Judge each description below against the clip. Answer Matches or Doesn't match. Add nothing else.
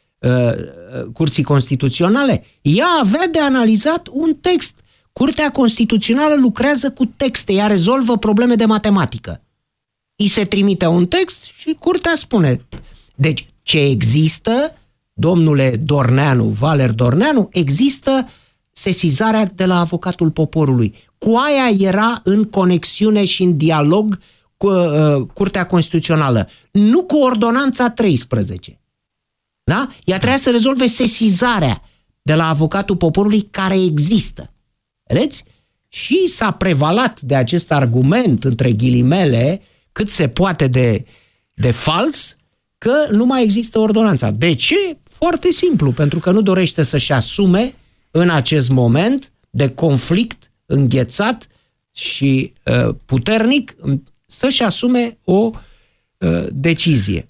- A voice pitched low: Doesn't match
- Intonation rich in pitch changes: Matches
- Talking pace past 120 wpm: Doesn't match